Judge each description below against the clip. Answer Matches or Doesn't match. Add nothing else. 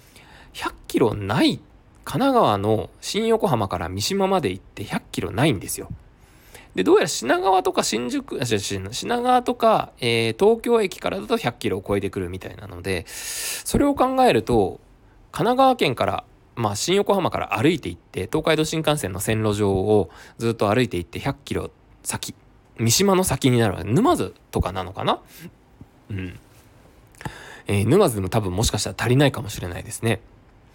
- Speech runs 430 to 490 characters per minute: Doesn't match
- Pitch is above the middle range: Doesn't match